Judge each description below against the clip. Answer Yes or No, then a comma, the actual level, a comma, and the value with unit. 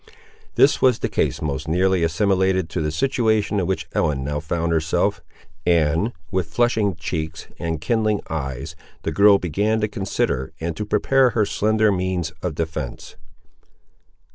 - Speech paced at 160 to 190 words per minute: No, average, 150 wpm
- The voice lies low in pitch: Yes, very low, 90 Hz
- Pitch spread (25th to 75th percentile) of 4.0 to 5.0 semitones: Yes, average, 4.7 semitones